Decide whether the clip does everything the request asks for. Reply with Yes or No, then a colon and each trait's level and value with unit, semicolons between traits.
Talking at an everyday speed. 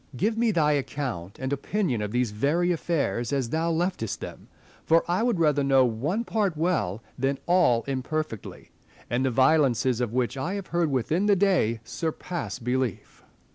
Yes: average, 170 wpm